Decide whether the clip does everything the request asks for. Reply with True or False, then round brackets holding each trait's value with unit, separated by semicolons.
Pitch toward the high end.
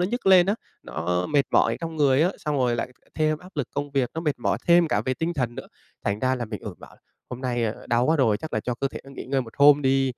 False (135 Hz)